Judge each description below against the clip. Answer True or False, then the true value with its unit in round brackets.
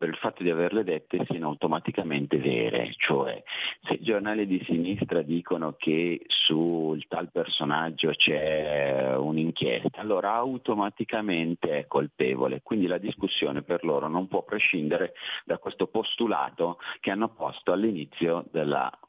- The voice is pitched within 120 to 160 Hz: False (85 Hz)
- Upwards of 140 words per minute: False (130 wpm)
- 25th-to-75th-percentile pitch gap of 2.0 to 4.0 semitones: True (3.6 semitones)